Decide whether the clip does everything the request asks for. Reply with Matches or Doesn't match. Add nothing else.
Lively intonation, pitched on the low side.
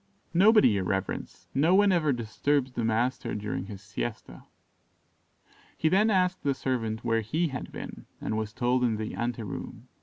Matches